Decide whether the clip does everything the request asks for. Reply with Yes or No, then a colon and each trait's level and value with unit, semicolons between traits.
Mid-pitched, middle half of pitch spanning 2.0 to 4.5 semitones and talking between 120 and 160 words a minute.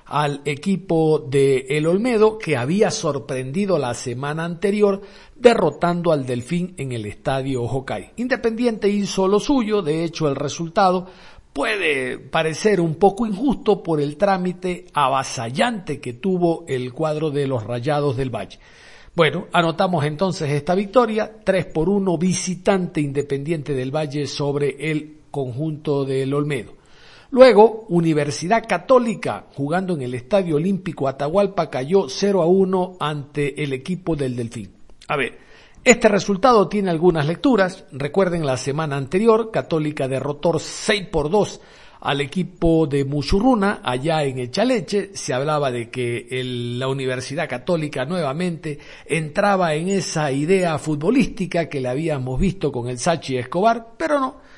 No: medium, 165 Hz; wide, 5.5 semitones; average, 140 wpm